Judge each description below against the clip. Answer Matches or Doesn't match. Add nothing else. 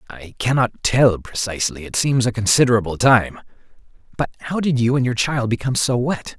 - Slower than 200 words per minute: Matches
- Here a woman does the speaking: Doesn't match